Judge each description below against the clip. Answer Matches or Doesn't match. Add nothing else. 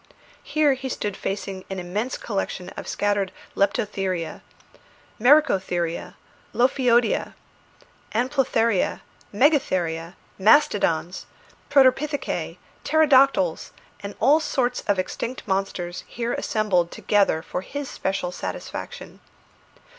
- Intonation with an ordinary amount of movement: Doesn't match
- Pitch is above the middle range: Matches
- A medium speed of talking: Doesn't match